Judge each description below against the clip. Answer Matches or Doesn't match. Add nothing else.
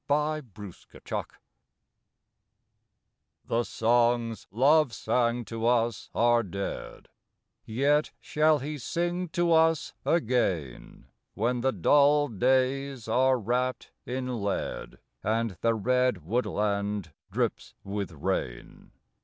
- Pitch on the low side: Matches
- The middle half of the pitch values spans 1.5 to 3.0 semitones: Doesn't match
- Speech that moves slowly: Matches